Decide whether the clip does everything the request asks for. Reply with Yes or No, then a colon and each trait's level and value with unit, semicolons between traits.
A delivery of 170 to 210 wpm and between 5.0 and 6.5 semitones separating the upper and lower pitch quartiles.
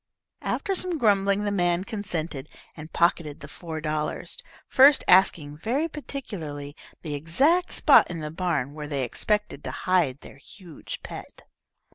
No: average, 145 wpm; wide, 5.5 semitones